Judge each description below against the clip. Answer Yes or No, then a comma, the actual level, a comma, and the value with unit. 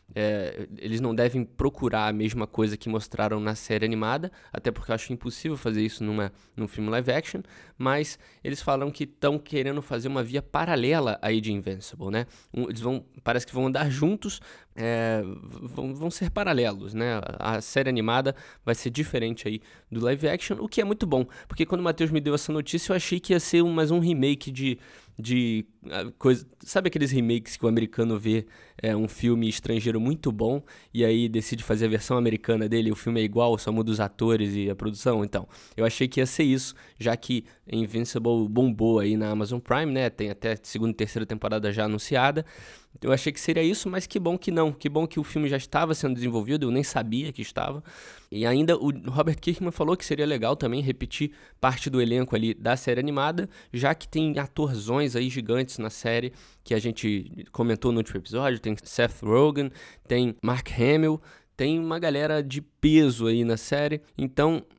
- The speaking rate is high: Yes, fast, 200 wpm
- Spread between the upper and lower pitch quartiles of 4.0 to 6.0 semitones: Yes, average, 4.7 semitones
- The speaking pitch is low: Yes, low, 125 Hz